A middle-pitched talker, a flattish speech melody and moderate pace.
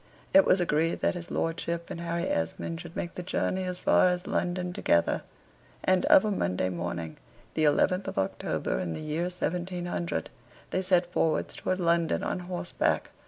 Yes: medium, 175 Hz; narrow, 2.1 semitones; average, 170 wpm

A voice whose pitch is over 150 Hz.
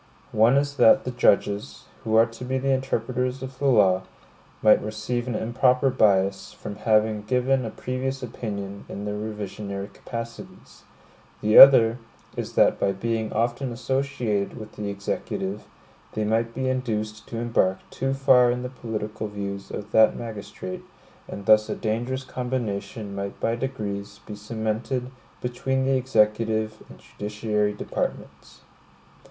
No: low, 110 Hz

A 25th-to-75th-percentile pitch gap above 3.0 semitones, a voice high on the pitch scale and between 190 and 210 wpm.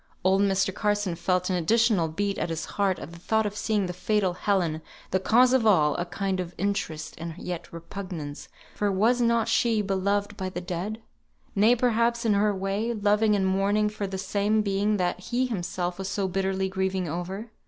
No: narrow, 2.6 semitones; high, 195 Hz; average, 195 wpm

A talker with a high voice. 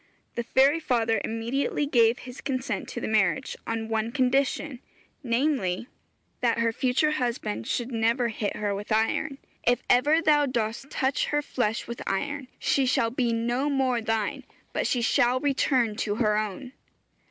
Yes: high, 245 Hz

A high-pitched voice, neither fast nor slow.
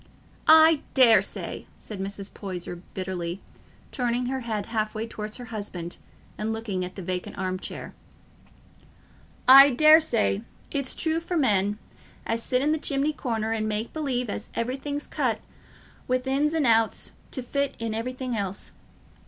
Yes: high, 230 Hz; average, 145 wpm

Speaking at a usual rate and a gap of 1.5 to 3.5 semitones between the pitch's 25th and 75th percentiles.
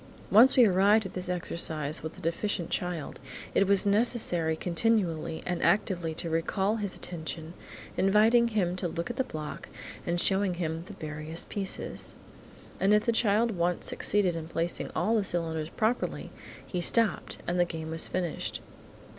No: average, 165 wpm; average, 3.9 semitones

